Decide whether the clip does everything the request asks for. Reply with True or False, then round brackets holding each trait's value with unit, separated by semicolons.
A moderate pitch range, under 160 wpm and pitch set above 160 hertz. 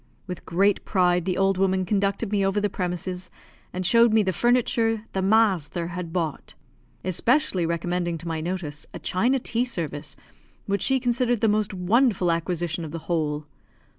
False (3.9 semitones; 165 wpm; 185 Hz)